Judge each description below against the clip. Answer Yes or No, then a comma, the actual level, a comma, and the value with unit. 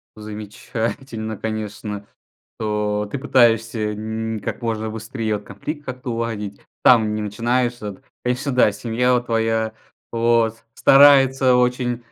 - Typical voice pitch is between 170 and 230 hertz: No, low, 115 Hz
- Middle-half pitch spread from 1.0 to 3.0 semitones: Yes, narrow, 2.5 semitones